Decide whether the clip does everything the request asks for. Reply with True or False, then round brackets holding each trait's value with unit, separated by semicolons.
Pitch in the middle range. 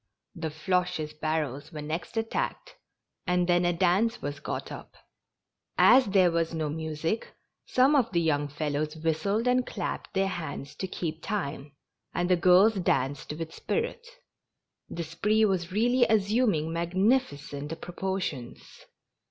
True (175 Hz)